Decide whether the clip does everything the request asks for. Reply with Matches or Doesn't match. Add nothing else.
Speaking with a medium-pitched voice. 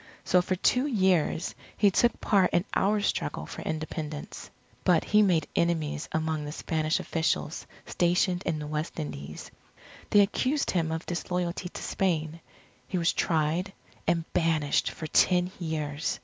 Matches